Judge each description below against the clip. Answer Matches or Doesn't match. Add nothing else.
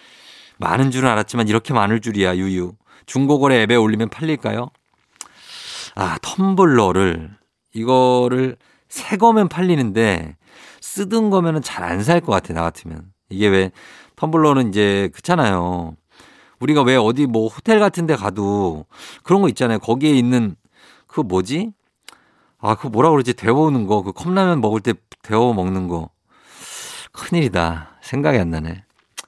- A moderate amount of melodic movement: Doesn't match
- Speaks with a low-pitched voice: Matches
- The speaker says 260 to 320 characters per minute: Matches